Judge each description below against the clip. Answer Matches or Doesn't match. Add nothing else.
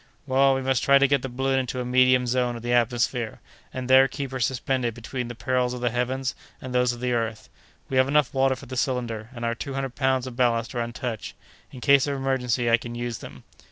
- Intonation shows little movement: Matches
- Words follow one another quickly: Matches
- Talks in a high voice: Doesn't match